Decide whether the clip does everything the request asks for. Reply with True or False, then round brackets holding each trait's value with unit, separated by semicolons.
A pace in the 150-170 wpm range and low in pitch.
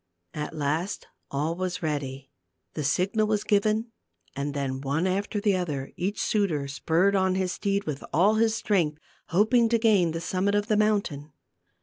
False (165 wpm; 185 Hz)